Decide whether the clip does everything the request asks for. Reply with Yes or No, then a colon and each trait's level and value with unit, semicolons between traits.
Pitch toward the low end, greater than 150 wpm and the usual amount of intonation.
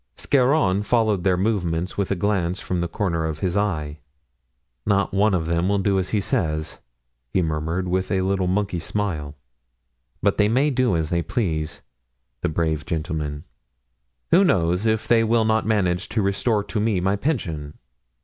Yes: very low, 95 Hz; average, 170 wpm; average, 4.0 semitones